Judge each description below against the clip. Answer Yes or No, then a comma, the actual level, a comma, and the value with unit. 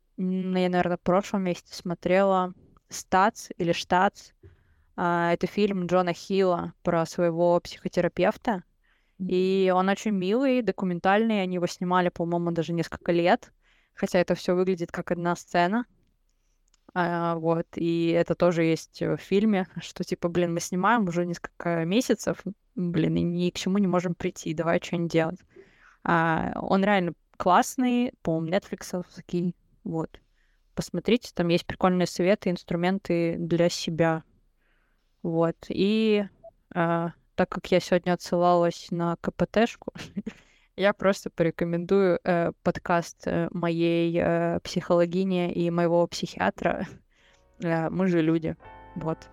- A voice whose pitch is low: No, medium, 175 Hz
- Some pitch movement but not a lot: No, narrow, 1.9 semitones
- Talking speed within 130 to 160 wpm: No, average, 120 wpm